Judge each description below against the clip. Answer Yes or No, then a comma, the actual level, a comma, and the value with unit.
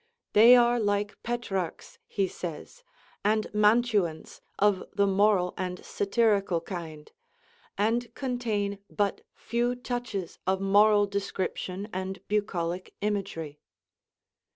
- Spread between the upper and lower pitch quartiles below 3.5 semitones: Yes, average, 2.8 semitones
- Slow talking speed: Yes, slow, 105 wpm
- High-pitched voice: Yes, high, 205 Hz